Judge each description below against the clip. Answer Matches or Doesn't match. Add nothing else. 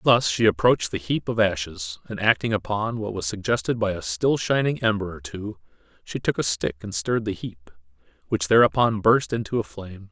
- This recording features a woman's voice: Doesn't match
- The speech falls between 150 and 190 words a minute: Doesn't match